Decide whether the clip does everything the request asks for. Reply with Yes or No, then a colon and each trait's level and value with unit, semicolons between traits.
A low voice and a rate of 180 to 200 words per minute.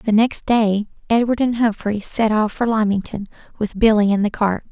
No: high, 215 Hz; average, 190 wpm